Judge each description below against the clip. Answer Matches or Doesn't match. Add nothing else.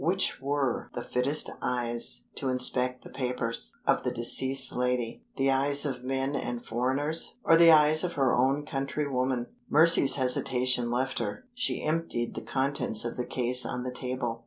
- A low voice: Matches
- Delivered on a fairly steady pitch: Matches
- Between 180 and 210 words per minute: Doesn't match